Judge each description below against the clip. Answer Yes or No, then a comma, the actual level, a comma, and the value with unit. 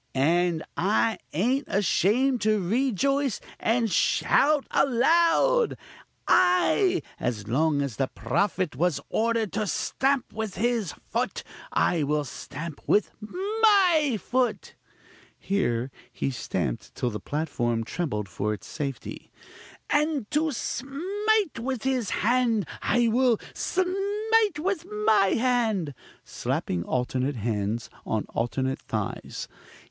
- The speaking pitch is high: Yes, high, 220 Hz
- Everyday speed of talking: No, slow, 115 wpm